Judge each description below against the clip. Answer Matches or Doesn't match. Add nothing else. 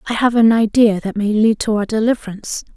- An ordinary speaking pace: Doesn't match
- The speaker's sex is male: Doesn't match